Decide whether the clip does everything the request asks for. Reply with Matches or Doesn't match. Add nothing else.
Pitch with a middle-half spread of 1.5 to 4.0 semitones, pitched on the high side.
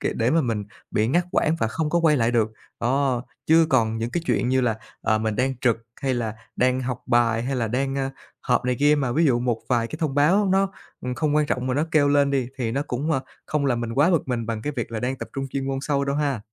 Doesn't match